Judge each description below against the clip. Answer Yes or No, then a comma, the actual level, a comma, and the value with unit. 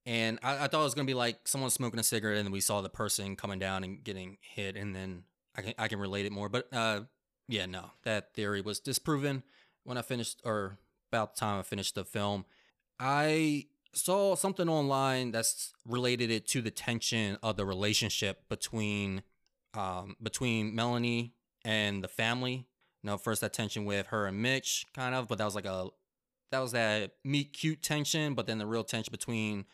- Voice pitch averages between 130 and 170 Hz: No, low, 115 Hz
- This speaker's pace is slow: No, average, 200 wpm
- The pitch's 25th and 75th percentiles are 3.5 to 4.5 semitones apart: Yes, average, 3.8 semitones